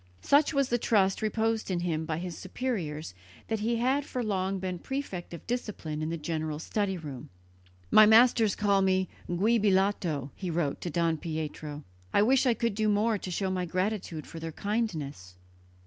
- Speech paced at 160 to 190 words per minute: Yes, average, 180 wpm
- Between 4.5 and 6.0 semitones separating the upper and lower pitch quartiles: Yes, average, 5.2 semitones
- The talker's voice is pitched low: No, high, 190 Hz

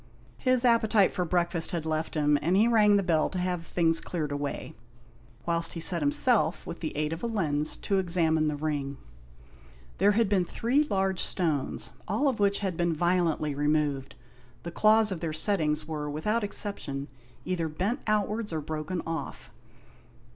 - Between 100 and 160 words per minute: No, average, 175 wpm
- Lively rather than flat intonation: No, average, 4.8 semitones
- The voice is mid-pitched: Yes, medium, 170 Hz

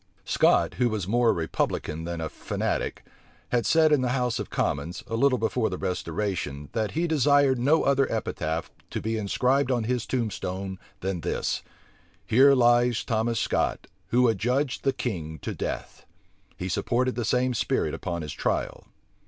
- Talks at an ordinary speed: Yes, average, 165 wpm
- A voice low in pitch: Yes, low, 115 Hz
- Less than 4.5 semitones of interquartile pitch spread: No, average, 5.3 semitones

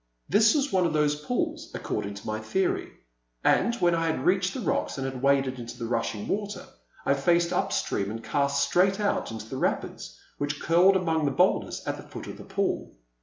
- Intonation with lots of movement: Yes, wide, 6.5 semitones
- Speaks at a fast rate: Yes, fast, 210 wpm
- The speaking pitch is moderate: Yes, medium, 150 Hz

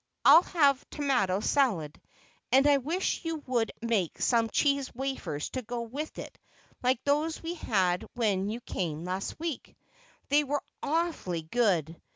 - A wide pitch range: Yes, wide, 7.0 semitones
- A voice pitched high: Yes, very high, 250 Hz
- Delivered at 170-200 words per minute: No, average, 150 wpm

